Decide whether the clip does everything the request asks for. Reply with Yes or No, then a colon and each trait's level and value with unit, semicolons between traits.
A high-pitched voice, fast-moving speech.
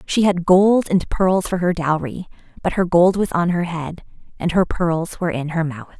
No: medium, 175 Hz; fast, 220 wpm